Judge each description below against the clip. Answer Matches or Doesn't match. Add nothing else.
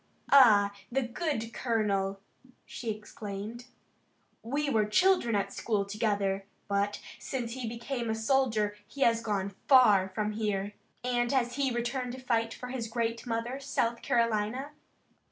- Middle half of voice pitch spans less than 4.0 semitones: Matches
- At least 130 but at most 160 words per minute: Matches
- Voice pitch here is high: Matches